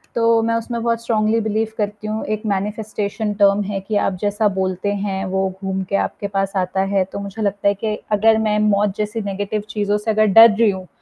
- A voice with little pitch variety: Yes, narrow, 1.8 semitones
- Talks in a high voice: Yes, high, 210 Hz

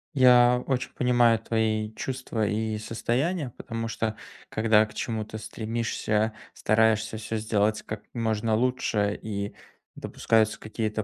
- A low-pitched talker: Yes, low, 110 Hz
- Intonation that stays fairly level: Yes, narrow, 1.5 semitones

